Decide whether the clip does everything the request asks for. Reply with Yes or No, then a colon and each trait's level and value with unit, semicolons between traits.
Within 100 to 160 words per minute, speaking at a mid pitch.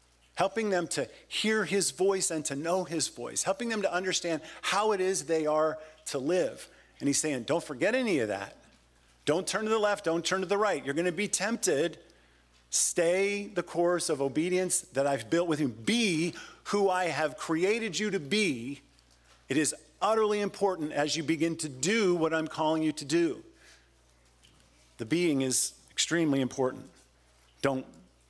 No: average, 180 wpm; medium, 165 Hz